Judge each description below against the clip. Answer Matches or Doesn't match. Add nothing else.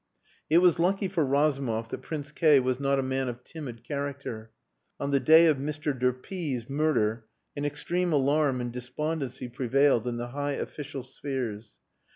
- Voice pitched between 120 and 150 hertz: Matches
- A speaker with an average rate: Matches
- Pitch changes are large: Doesn't match